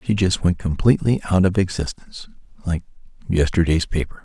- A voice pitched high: No, very low, 90 Hz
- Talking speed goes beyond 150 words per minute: No, average, 140 wpm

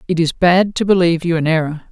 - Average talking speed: No, fast, 250 wpm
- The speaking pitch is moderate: Yes, medium, 170 Hz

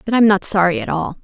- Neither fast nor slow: No, fast, 290 wpm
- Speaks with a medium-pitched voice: No, high, 200 Hz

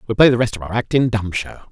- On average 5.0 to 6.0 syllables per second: No, 6.8 syllables/s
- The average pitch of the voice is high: No, low, 110 Hz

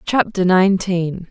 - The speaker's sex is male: No, female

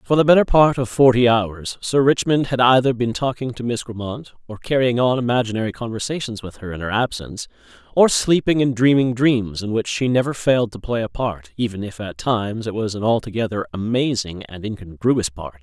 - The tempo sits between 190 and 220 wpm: Yes, average, 200 wpm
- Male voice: Yes, male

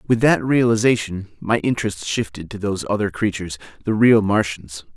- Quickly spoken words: No, average, 155 wpm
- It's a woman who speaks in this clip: No, male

